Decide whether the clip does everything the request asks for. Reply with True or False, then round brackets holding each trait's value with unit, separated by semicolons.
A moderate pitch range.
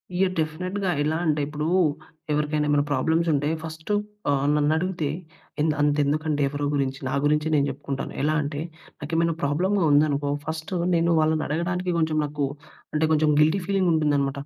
False (2.1 semitones)